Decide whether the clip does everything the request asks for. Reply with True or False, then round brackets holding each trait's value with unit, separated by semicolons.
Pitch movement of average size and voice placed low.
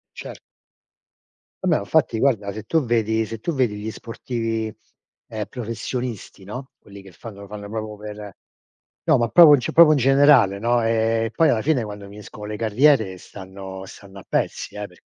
True (3.2 semitones; 110 Hz)